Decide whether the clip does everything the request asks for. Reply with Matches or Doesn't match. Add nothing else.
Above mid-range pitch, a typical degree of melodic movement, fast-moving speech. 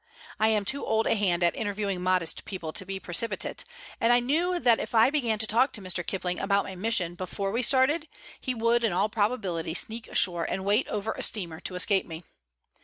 Matches